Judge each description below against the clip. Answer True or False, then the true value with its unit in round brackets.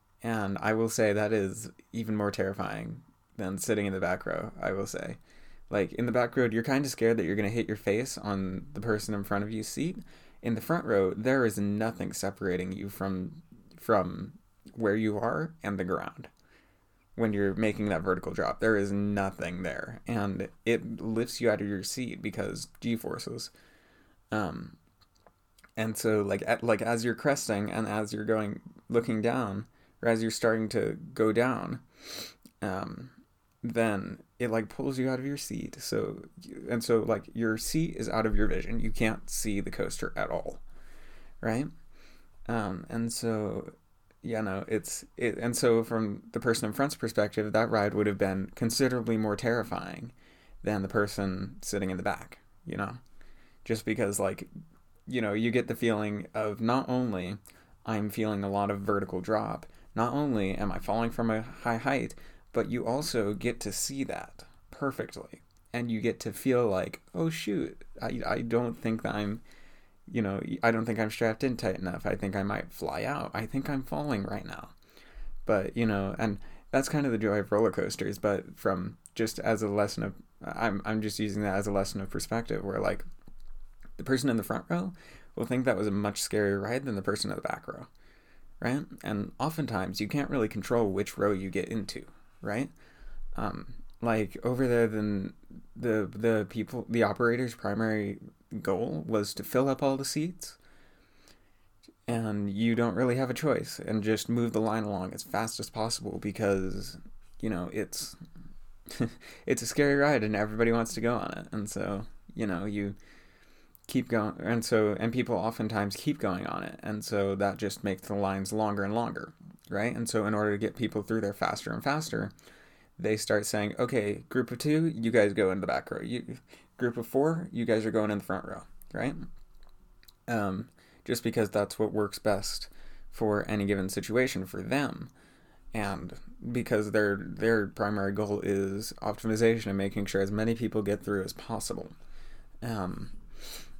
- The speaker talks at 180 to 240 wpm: True (190 wpm)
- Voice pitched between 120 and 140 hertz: False (110 Hz)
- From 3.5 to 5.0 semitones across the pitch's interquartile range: False (2.6 semitones)